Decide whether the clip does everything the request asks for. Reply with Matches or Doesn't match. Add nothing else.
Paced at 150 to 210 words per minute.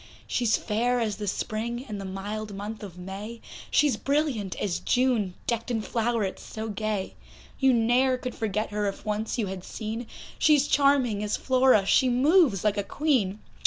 Matches